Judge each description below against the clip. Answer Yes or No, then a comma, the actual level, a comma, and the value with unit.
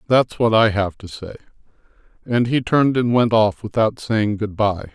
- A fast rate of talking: No, average, 195 wpm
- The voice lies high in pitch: No, low, 110 Hz